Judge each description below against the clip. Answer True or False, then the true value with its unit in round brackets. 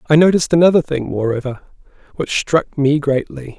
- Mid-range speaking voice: True (145 Hz)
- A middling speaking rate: True (150 wpm)